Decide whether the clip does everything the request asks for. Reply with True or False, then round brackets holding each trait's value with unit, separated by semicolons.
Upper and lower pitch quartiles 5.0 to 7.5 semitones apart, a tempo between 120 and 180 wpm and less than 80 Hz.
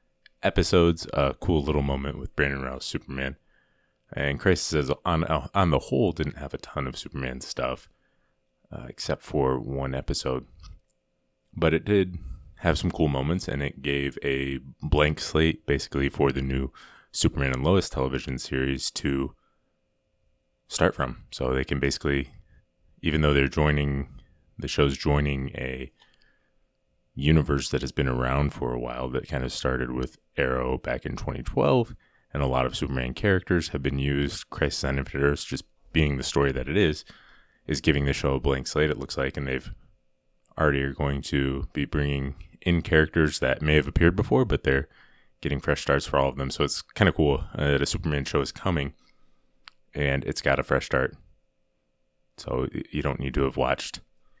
False (2.7 semitones; 175 wpm; 70 Hz)